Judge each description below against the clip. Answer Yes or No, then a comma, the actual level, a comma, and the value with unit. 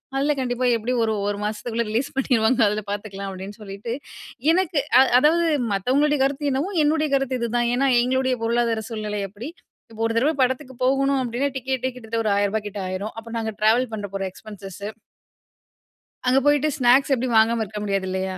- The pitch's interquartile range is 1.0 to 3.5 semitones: No, average, 3.9 semitones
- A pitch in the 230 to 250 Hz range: Yes, high, 235 Hz